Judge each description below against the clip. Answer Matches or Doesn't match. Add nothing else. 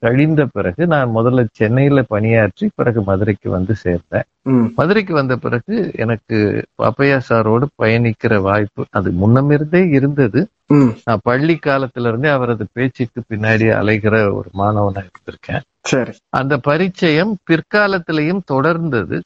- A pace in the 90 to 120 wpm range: Matches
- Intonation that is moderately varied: Matches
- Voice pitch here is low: Matches